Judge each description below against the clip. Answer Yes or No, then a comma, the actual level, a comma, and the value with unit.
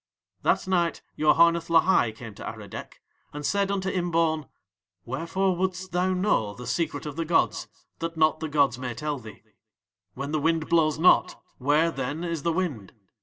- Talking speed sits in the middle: Yes, average, 170 wpm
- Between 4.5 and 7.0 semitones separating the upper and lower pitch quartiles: No, average, 3.5 semitones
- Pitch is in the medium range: Yes, medium, 160 Hz